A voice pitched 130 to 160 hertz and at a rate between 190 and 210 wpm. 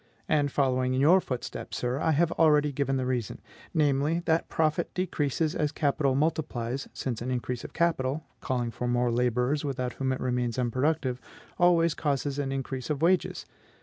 No: low, 135 Hz; average, 170 wpm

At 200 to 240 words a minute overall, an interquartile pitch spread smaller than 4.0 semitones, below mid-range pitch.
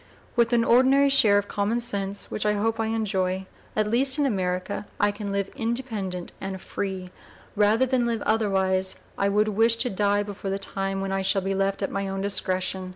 No: fast, 205 wpm; average, 2.7 semitones; high, 205 Hz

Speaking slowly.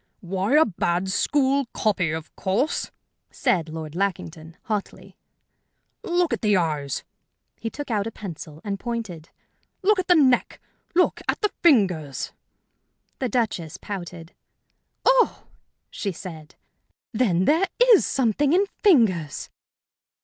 Yes: slow, 125 wpm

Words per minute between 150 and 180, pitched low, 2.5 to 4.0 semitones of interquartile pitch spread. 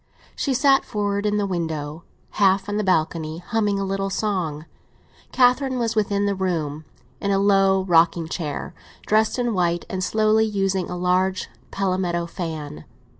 No: average, 155 wpm; high, 190 Hz; average, 3.3 semitones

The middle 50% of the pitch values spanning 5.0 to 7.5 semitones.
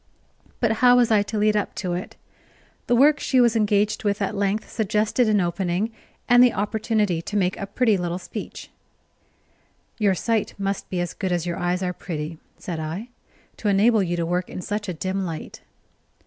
No: average, 3.4 semitones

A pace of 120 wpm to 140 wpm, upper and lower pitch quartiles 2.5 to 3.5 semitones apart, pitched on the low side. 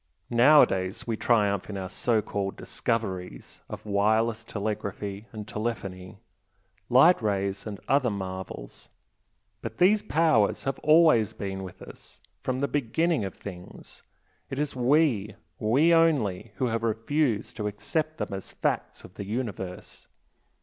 No: slow, 135 wpm; average, 4.9 semitones; low, 110 Hz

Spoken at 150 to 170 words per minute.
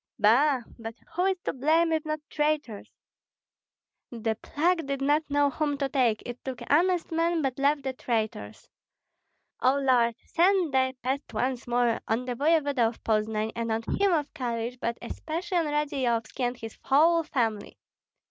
Yes: average, 165 wpm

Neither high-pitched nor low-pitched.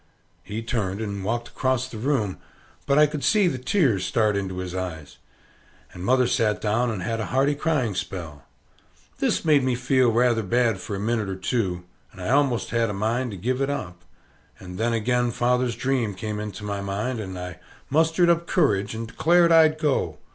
No: low, 115 Hz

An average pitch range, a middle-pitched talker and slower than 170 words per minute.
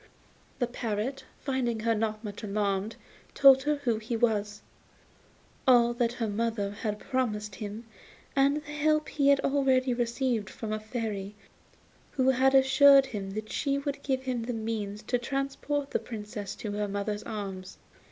No: average, 4.1 semitones; high, 235 Hz; average, 160 wpm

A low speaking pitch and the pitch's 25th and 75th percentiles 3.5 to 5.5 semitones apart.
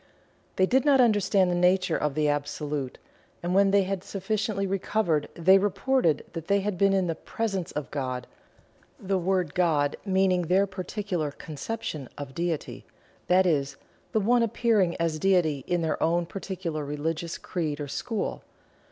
No: medium, 180 Hz; average, 4.2 semitones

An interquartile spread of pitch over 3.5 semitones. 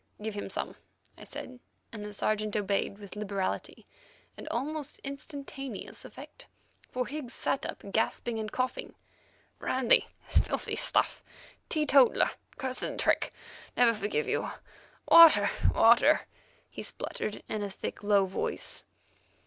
Yes: average, 4.6 semitones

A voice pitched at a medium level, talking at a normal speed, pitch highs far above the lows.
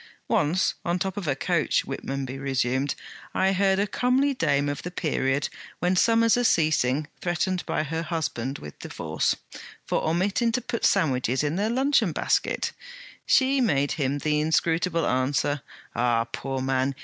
Yes: medium, 155 Hz; average, 160 wpm; wide, 5.9 semitones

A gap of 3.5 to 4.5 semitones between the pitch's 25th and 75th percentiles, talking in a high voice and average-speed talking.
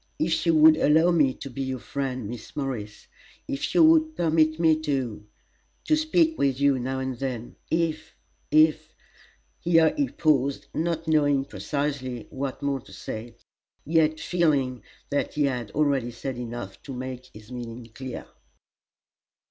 No: average, 3.8 semitones; medium, 140 Hz; average, 155 wpm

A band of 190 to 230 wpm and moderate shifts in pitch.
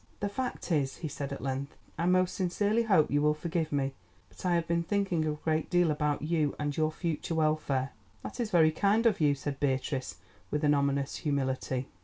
Yes: fast, 205 wpm; average, 3.6 semitones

